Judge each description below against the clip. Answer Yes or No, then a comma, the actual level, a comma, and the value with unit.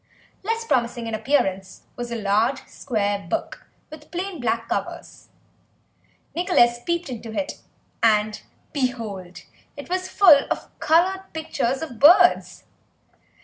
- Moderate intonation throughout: No, wide, 7.2 semitones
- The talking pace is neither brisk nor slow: No, slow, 120 wpm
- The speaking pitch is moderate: No, very high, 260 Hz